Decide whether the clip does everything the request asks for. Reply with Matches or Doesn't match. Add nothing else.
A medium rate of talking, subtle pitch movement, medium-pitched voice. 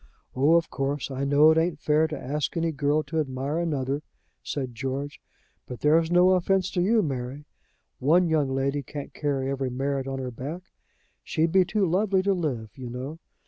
Doesn't match